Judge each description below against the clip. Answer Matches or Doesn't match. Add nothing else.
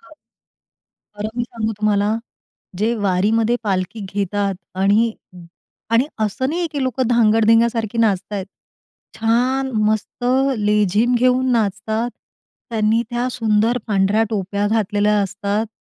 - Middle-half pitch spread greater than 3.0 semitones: Doesn't match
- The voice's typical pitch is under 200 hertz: Doesn't match